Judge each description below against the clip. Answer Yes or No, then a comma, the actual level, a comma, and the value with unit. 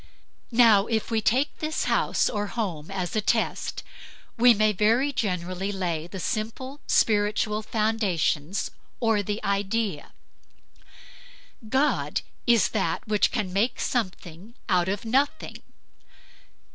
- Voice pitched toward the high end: Yes, high, 210 Hz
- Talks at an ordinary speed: No, slow, 120 wpm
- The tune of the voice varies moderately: Yes, average, 3.2 semitones